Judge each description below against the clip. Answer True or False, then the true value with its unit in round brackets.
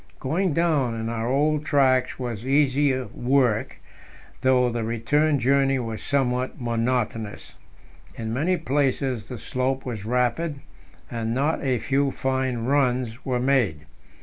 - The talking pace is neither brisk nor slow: False (130 wpm)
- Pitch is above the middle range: False (130 Hz)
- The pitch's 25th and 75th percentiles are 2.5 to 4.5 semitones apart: True (2.9 semitones)